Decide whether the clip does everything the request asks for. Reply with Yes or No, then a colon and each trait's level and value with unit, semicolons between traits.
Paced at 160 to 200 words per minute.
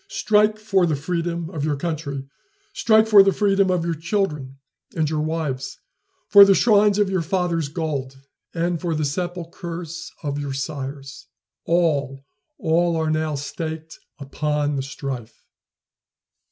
No: average, 145 wpm